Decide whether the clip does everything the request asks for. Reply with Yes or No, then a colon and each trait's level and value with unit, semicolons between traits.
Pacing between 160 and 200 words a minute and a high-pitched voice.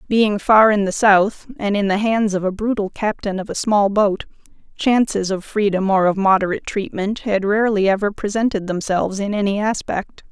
Yes: average, 185 wpm; high, 205 Hz